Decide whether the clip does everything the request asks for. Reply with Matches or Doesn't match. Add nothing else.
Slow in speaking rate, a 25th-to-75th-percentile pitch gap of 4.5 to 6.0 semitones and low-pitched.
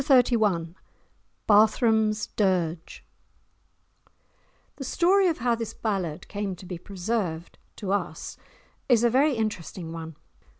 Doesn't match